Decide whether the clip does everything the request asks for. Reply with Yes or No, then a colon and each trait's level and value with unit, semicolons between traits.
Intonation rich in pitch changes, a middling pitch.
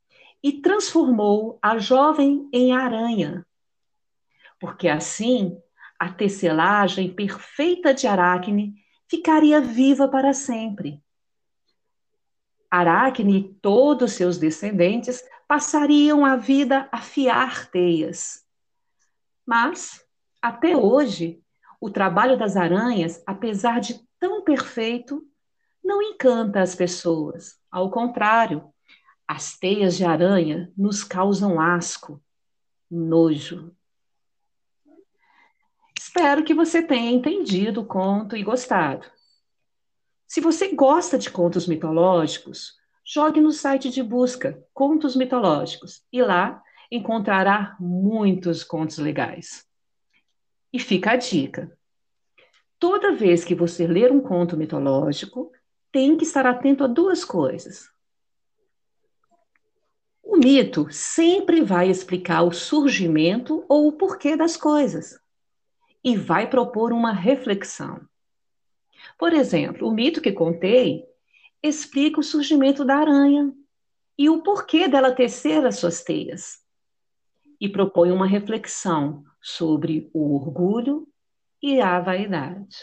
No: wide, 8.4 semitones; high, 240 Hz